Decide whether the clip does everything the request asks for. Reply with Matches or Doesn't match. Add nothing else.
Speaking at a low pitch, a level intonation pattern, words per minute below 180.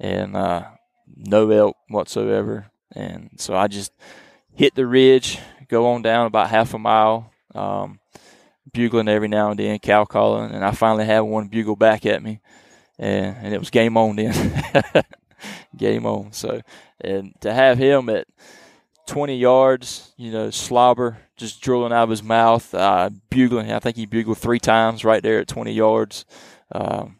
Matches